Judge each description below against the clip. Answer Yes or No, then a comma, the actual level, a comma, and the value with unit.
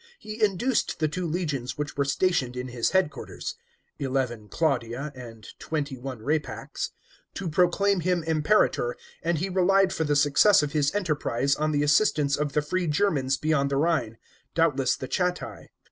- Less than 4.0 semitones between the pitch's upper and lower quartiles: No, average, 4.5 semitones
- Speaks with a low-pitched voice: No, medium, 150 Hz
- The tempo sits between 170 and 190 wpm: No, average, 160 wpm